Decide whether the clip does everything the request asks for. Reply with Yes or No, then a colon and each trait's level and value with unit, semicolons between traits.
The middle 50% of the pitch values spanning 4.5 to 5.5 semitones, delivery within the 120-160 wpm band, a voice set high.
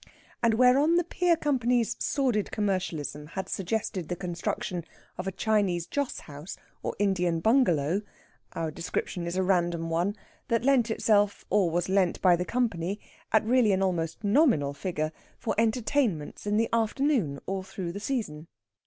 Yes: average, 5.1 semitones; average, 155 wpm; high, 195 Hz